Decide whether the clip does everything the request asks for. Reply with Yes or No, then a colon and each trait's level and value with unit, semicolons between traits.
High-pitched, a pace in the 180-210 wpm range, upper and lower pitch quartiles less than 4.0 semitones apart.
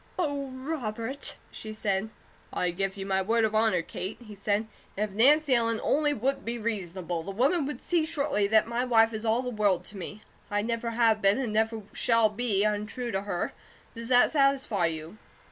Yes: high, 220 Hz; average, 195 wpm; average, 3.4 semitones